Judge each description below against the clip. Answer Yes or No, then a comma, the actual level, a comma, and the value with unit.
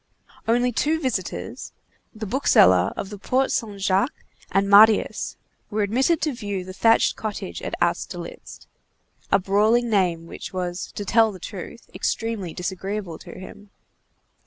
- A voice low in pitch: No, high, 205 Hz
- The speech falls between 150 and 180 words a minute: No, average, 140 wpm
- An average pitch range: Yes, average, 3.4 semitones